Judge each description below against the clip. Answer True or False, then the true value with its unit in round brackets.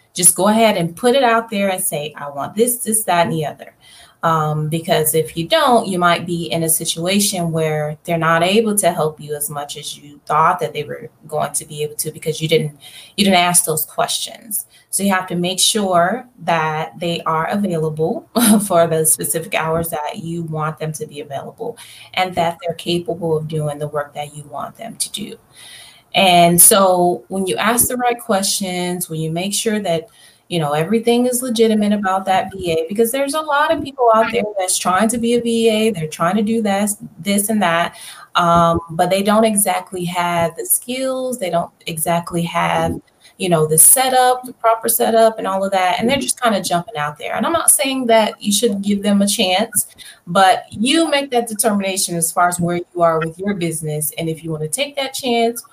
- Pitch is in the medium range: True (180 Hz)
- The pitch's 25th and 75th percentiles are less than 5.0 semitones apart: False (5.5 semitones)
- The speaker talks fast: True (215 wpm)